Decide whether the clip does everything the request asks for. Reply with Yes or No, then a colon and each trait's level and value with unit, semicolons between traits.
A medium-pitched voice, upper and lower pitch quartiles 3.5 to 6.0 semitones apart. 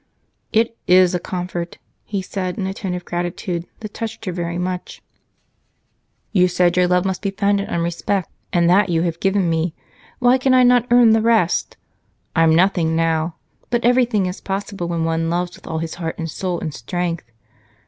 No: medium, 180 Hz; average, 2.9 semitones